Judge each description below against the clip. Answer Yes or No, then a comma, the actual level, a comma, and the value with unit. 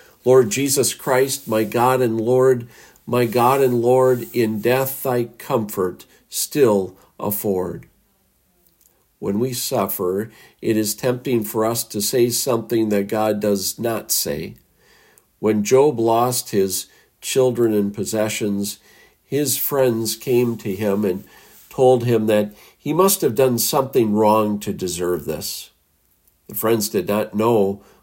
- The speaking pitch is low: Yes, low, 115 Hz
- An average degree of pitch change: Yes, average, 3.4 semitones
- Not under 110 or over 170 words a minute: Yes, slow, 135 wpm